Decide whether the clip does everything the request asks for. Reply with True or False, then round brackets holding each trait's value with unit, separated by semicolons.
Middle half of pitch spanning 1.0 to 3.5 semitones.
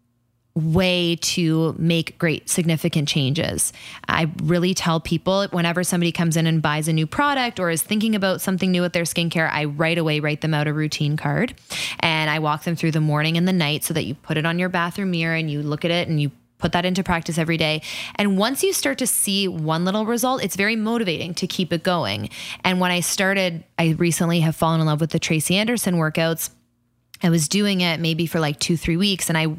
True (2.5 semitones)